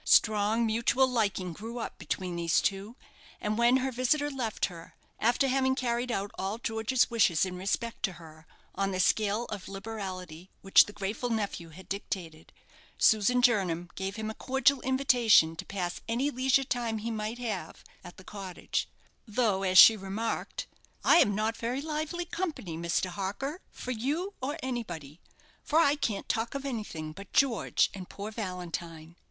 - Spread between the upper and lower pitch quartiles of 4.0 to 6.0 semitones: Yes, average, 4.7 semitones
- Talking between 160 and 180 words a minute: Yes, average, 165 wpm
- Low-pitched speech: No, high, 215 Hz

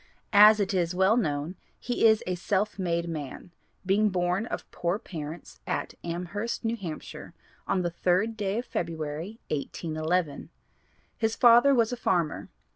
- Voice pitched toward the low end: No, medium, 185 Hz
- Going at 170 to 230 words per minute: No, average, 150 wpm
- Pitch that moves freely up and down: No, average, 4.4 semitones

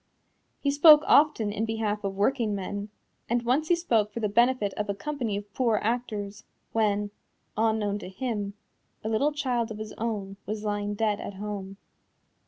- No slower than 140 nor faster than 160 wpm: No, average, 170 wpm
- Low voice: No, high, 215 Hz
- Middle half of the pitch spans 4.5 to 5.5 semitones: No, average, 2.8 semitones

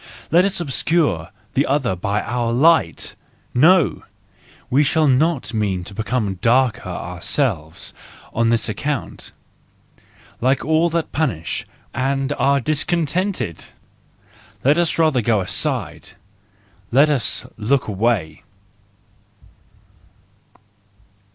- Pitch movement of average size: No, wide, 6.2 semitones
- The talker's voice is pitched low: Yes, low, 130 Hz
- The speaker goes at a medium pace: No, slow, 100 wpm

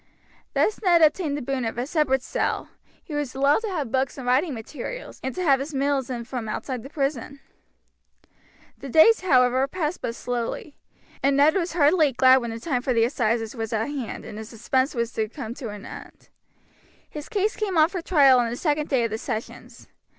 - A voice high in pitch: Yes, very high, 270 Hz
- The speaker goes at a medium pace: No, fast, 210 wpm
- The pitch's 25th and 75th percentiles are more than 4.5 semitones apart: No, average, 4.2 semitones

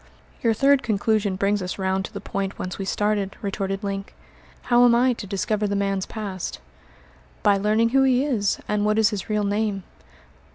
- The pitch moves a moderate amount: No, narrow, 2.1 semitones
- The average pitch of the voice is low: No, high, 205 Hz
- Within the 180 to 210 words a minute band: Yes, average, 190 wpm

